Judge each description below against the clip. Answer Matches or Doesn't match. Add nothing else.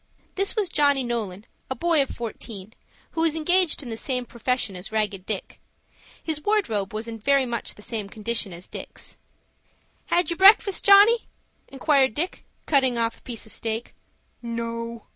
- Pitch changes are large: Matches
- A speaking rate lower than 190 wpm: Matches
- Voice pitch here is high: Matches